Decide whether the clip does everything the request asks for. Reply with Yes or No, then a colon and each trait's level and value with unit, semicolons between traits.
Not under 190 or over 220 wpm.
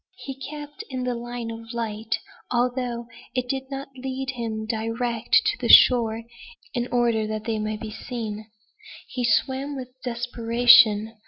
No: average, 150 wpm